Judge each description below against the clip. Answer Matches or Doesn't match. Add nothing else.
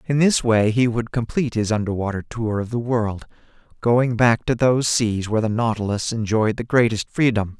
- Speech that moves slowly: Doesn't match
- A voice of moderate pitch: Doesn't match